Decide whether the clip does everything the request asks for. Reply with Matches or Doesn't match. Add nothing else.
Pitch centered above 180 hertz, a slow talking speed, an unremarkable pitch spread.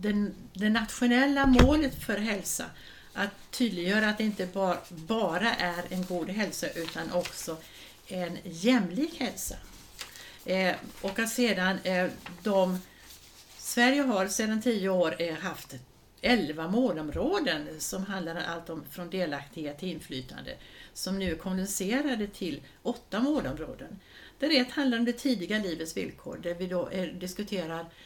Matches